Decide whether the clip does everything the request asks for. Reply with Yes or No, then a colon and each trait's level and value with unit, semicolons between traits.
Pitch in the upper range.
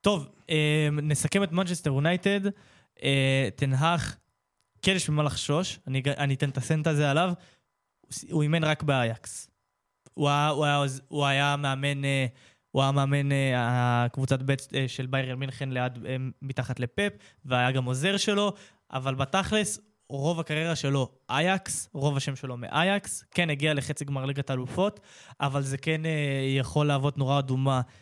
No: medium, 140 Hz